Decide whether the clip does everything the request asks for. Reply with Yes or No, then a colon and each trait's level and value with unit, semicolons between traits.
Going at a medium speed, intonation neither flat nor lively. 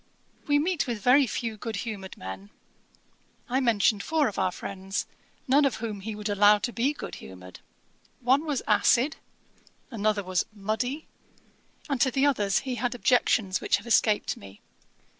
Yes: average, 160 wpm; average, 4.4 semitones